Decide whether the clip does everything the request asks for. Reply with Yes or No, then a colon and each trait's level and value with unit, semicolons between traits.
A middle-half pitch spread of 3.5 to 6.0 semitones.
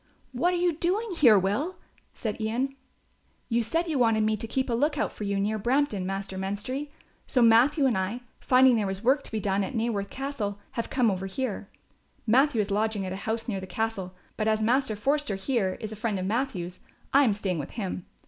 Yes: average, 4.9 semitones